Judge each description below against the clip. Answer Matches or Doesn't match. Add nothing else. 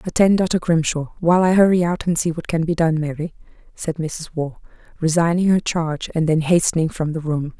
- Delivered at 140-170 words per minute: Doesn't match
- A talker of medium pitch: Matches